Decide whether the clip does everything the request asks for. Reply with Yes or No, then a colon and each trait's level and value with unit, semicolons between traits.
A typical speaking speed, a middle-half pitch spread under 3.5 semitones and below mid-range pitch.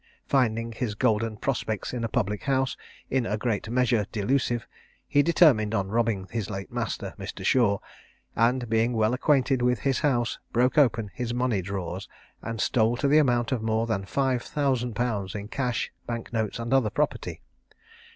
Yes: average, 170 wpm; average, 2.9 semitones; low, 115 Hz